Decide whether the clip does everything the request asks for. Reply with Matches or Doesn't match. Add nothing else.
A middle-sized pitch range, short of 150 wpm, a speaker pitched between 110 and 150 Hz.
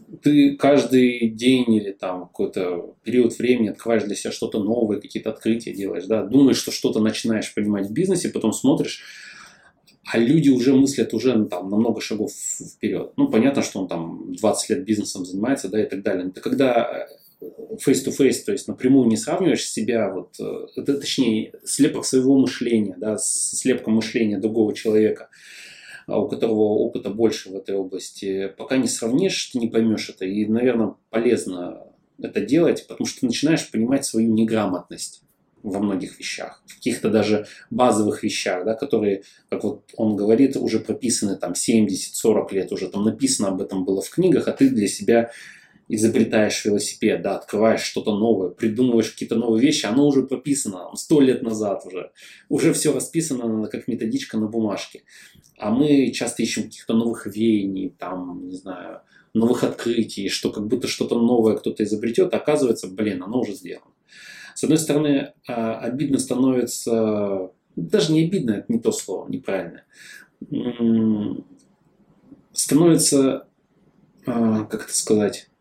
Doesn't match